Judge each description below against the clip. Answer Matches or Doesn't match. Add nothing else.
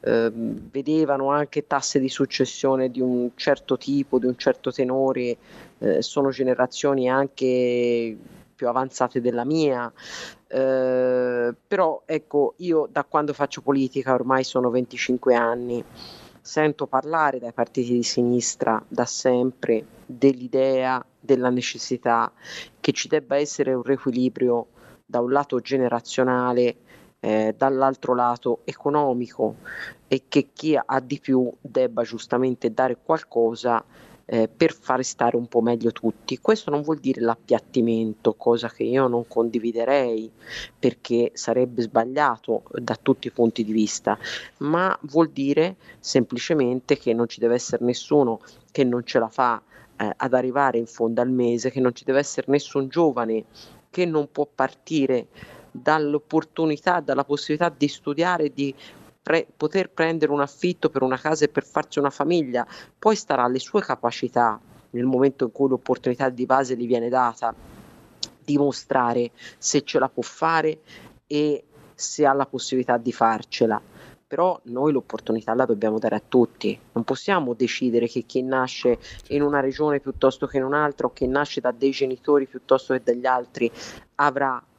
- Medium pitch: Doesn't match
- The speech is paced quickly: Doesn't match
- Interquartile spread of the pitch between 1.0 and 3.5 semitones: Matches